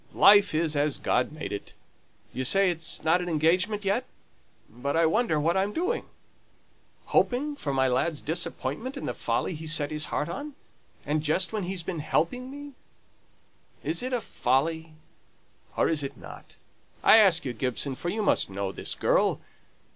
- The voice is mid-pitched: Yes, medium, 165 Hz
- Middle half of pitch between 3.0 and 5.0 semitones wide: No, wide, 5.6 semitones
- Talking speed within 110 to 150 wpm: No, average, 175 wpm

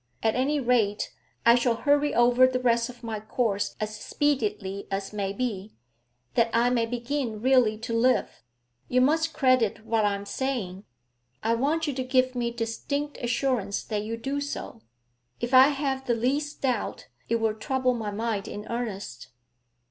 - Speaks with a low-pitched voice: No, high, 235 Hz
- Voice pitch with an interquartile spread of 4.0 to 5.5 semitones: No, average, 3.3 semitones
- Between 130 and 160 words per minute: No, average, 170 wpm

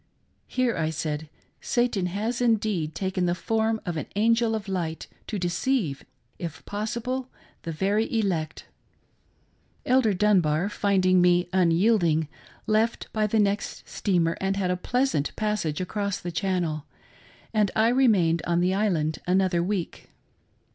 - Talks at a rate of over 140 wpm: No, slow, 135 wpm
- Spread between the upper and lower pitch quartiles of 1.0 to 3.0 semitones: No, average, 4.2 semitones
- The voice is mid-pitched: No, high, 195 Hz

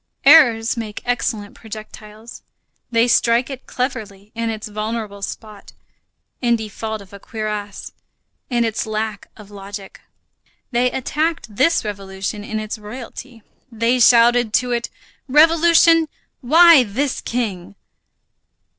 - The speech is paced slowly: Yes, slow, 120 wpm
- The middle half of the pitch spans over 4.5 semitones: No, average, 2.8 semitones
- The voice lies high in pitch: Yes, high, 225 Hz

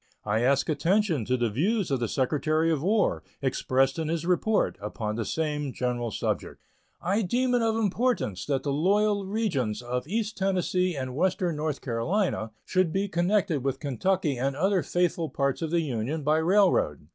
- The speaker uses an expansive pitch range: Yes, wide, 6.5 semitones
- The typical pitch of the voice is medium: Yes, medium, 160 Hz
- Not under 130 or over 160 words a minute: No, average, 175 wpm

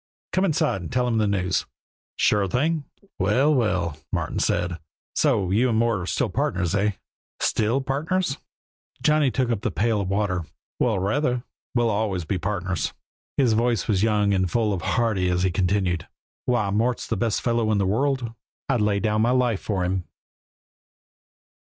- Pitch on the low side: Yes, low, 105 Hz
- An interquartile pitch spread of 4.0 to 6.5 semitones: Yes, average, 4.4 semitones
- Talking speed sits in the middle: Yes, average, 170 wpm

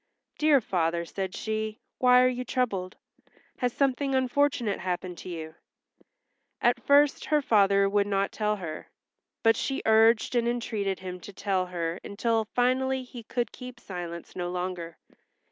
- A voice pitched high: Yes, high, 215 Hz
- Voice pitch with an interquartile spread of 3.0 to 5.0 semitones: No, wide, 5.4 semitones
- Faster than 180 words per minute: No, average, 150 wpm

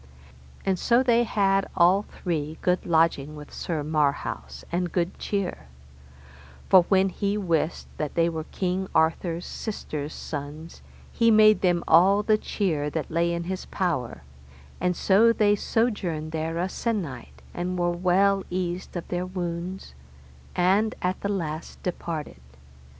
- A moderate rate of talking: Yes, average, 145 wpm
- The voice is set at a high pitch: No, medium, 175 Hz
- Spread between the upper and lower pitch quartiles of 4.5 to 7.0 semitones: No, average, 3.3 semitones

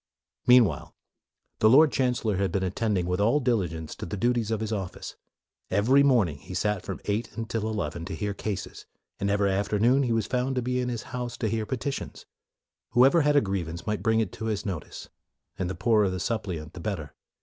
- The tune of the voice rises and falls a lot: No, average, 4.2 semitones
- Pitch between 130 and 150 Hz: No, low, 105 Hz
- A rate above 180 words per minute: Yes, average, 200 wpm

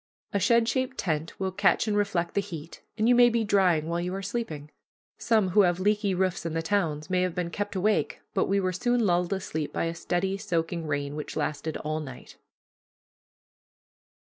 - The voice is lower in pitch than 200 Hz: Yes, medium, 185 Hz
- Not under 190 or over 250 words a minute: Yes, average, 195 wpm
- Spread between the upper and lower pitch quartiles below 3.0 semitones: No, average, 3.8 semitones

